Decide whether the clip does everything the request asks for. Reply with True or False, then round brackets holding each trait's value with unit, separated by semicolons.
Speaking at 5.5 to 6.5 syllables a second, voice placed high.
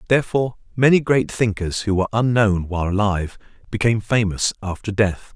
False (6.0 syllables/s; 105 Hz)